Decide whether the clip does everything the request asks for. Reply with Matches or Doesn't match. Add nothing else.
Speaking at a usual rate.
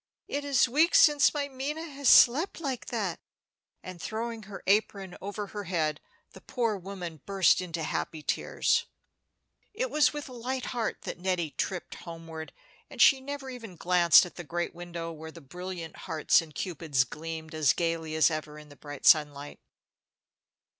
Matches